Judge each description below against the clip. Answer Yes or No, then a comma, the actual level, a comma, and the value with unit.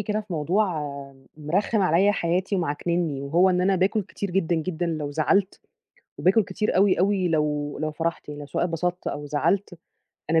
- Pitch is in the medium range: Yes, medium, 175 Hz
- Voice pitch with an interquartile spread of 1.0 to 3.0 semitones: No, average, 3.7 semitones